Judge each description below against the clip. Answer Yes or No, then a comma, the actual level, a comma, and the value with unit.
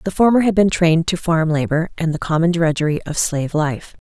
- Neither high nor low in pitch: Yes, medium, 165 Hz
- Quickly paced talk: Yes, fast, 220 wpm